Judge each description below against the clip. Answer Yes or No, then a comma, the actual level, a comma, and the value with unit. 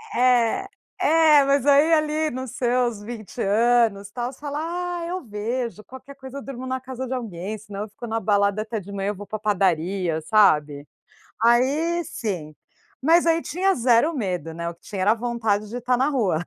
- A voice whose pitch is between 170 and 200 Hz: No, high, 235 Hz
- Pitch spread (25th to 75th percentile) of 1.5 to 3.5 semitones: No, average, 4.5 semitones